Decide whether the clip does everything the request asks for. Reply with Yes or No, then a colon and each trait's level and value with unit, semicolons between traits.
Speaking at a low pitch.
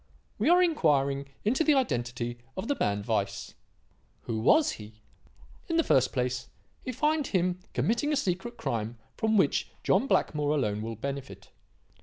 No: medium, 150 Hz